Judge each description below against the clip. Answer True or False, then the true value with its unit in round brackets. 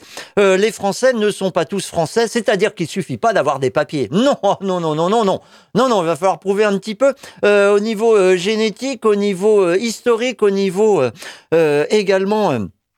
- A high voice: True (200 Hz)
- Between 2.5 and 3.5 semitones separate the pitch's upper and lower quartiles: True (3.2 semitones)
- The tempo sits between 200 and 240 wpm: True (215 wpm)